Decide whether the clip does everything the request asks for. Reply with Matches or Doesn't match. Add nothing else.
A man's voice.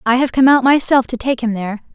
Doesn't match